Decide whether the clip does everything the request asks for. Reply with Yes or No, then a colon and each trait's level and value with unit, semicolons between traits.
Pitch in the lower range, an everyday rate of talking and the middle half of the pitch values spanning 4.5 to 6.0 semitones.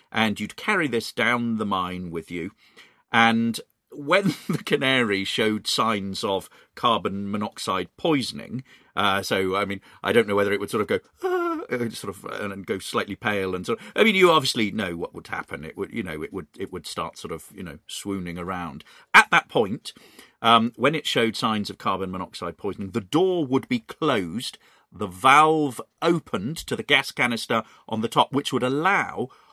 Yes: low, 115 Hz; average, 195 wpm; average, 5.2 semitones